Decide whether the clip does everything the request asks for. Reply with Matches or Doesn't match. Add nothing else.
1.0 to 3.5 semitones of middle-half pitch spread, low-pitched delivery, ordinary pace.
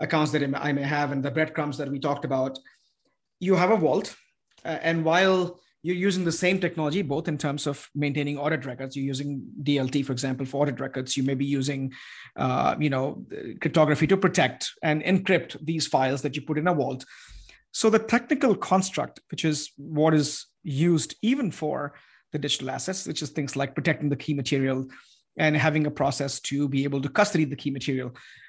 Doesn't match